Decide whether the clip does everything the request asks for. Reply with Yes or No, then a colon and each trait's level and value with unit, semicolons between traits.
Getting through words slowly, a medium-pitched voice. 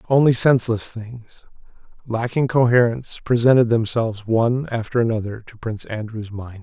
No: slow, 125 wpm; low, 115 Hz